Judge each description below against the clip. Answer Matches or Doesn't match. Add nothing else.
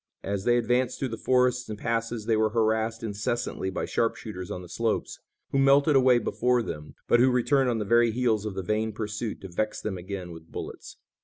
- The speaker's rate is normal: Doesn't match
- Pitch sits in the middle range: Doesn't match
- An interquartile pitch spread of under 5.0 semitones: Matches